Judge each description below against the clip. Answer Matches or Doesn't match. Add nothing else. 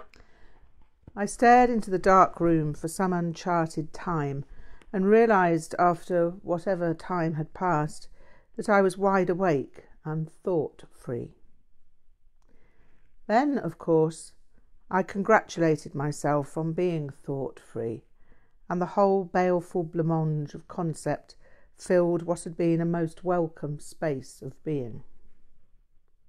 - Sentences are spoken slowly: Matches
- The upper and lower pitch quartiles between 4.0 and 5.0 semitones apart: Doesn't match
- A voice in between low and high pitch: Matches